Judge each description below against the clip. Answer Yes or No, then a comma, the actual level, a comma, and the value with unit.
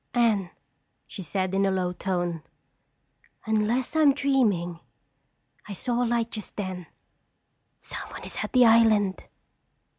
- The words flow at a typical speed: No, slow, 125 wpm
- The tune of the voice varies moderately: Yes, average, 4.1 semitones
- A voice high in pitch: Yes, high, 210 Hz